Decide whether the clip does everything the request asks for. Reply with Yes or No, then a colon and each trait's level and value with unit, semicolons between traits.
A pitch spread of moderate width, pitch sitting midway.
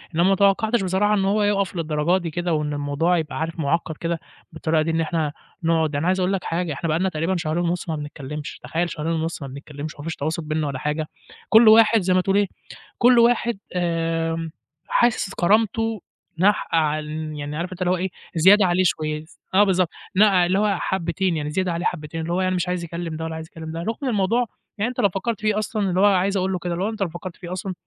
Yes: average, 3.3 semitones; medium, 175 Hz